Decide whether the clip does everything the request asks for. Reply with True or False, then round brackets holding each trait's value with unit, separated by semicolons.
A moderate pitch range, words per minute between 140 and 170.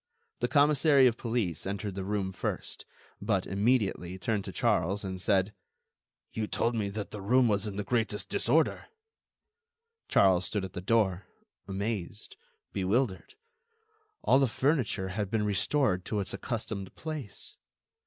True (3.4 semitones; 145 wpm)